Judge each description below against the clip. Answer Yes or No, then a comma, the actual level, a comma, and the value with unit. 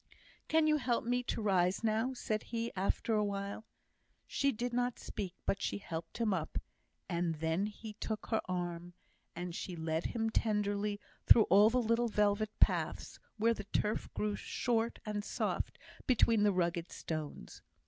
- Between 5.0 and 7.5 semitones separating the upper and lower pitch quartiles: No, average, 4.1 semitones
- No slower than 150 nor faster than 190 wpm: Yes, average, 165 wpm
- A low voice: No, high, 210 Hz